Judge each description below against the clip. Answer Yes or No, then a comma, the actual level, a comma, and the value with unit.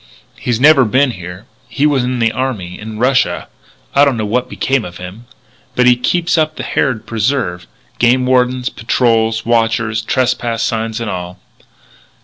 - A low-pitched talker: Yes, low, 120 Hz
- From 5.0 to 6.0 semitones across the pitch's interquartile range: No, narrow, 2.6 semitones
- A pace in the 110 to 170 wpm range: Yes, average, 160 wpm